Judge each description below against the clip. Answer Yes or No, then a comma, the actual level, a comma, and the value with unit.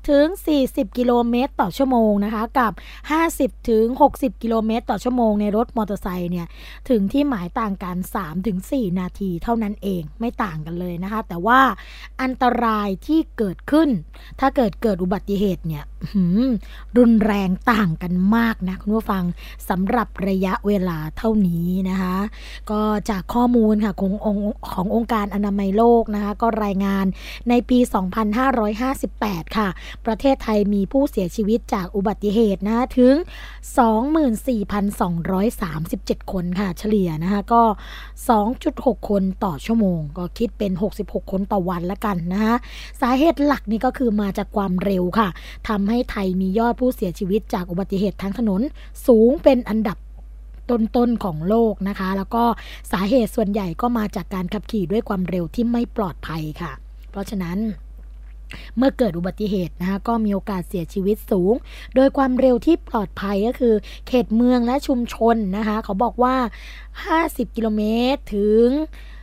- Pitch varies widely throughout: No, average, 3.8 semitones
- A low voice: No, high, 215 Hz